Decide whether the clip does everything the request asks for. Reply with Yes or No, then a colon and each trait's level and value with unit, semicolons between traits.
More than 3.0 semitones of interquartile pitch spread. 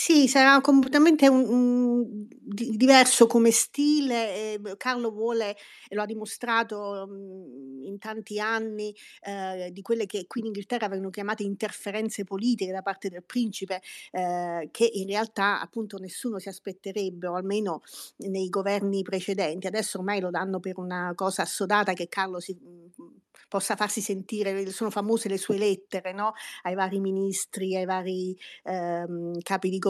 No: average, 2.7 semitones